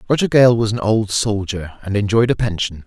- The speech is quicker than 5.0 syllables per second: Yes, 5.3 syllables/s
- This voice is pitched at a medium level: No, low, 110 Hz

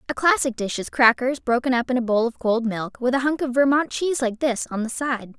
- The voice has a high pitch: Yes, very high, 250 Hz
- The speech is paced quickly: Yes, fast, 270 wpm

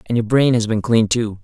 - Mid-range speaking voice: No, low, 115 Hz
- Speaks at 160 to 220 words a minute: No, fast, 295 wpm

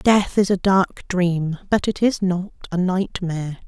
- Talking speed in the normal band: Yes, average, 180 wpm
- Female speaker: Yes, female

